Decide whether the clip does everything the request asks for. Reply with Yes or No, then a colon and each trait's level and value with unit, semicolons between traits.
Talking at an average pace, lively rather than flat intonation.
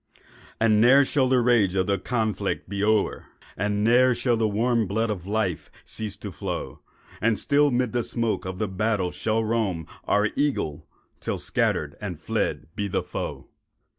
No: average, 165 wpm; average, 3.0 semitones